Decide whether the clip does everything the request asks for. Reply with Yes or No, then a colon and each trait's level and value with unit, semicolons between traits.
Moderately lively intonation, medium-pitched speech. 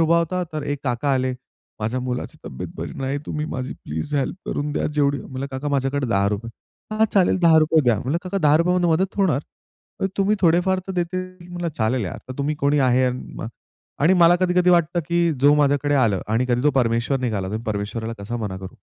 No: wide, 5.7 semitones; medium, 145 Hz